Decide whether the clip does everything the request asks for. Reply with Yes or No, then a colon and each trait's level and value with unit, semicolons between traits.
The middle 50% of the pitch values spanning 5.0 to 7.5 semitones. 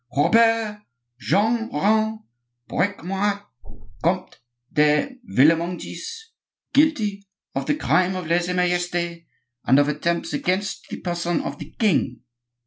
No: average, 4.4 semitones